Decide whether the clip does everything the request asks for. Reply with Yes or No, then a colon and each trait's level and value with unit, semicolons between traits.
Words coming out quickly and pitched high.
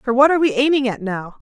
Yes: fast, 285 wpm; very high, 250 Hz